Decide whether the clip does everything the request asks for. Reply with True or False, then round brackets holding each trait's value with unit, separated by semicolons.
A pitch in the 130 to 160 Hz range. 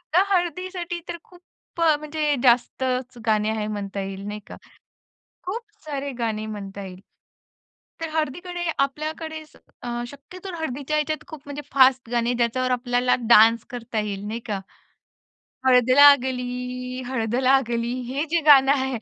False (255 Hz)